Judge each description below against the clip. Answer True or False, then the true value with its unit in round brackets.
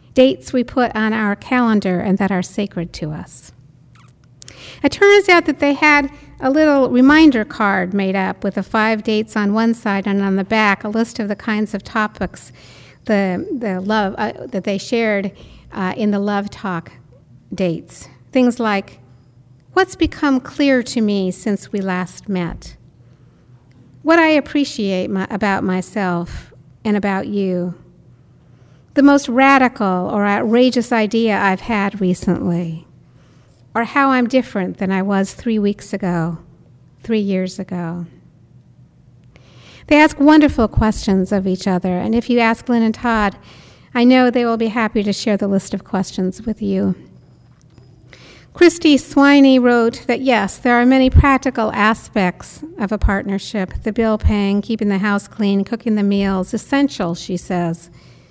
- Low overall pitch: False (205 Hz)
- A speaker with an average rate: True (155 wpm)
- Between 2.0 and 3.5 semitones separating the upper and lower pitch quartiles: False (4.4 semitones)